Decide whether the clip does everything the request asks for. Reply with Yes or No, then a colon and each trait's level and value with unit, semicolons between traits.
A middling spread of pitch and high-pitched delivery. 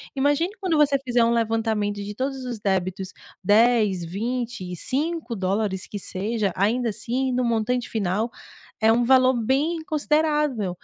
Yes: average, 4.3 semitones; high, 235 Hz